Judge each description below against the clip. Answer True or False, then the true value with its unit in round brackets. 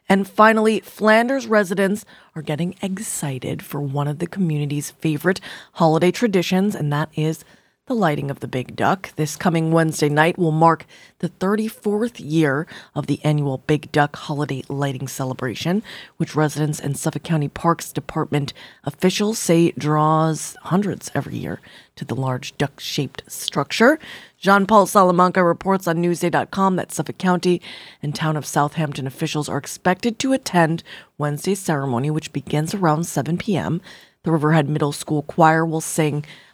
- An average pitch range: True (3.9 semitones)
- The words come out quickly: False (150 wpm)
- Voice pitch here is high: False (160 Hz)